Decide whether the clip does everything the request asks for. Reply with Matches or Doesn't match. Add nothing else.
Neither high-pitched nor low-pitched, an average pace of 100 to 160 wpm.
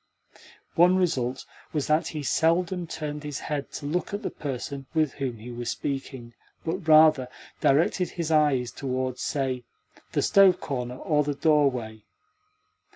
Matches